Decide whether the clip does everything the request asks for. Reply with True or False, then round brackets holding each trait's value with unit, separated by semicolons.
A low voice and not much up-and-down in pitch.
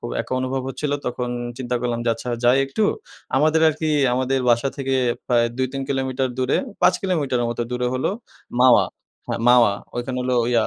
True (130 Hz; 1.8 semitones)